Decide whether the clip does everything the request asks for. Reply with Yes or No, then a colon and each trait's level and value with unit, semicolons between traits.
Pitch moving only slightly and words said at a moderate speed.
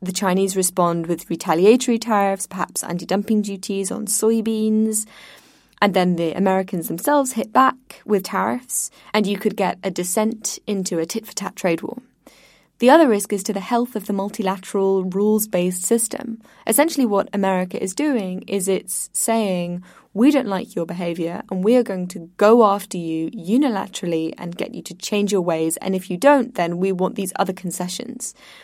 No: average, 3.5 semitones; average, 180 wpm